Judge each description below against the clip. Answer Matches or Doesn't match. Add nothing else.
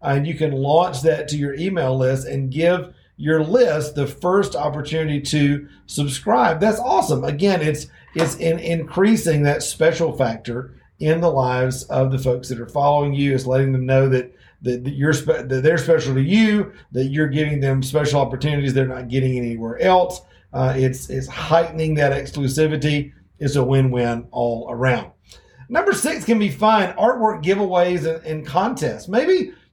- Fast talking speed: Doesn't match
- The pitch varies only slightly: Doesn't match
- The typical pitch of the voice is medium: Matches